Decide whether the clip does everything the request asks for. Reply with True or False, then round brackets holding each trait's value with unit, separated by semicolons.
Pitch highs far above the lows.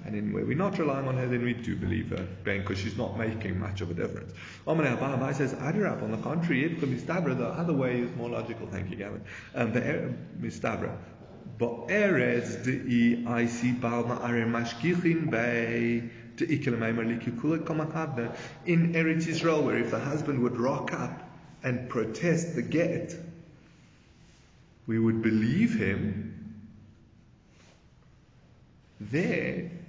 True (5.8 semitones)